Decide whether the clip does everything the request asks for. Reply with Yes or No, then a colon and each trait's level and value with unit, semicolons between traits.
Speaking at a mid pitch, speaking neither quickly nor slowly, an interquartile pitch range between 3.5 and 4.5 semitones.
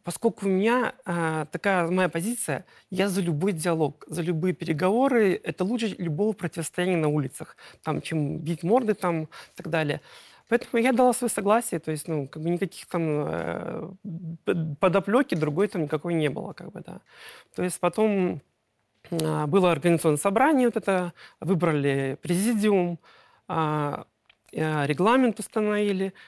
Yes: medium, 175 Hz; average, 135 wpm; average, 4.2 semitones